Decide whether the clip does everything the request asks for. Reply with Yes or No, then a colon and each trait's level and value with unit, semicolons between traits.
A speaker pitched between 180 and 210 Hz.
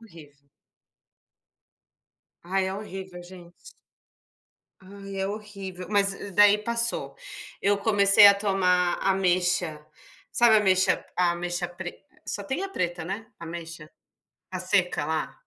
Yes: high, 190 Hz